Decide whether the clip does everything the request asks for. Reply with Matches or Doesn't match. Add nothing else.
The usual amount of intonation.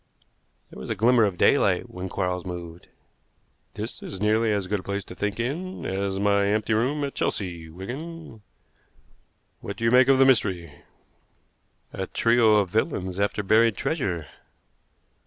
Matches